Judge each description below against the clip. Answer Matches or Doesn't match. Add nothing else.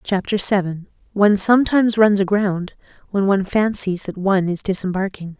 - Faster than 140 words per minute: Doesn't match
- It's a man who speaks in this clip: Doesn't match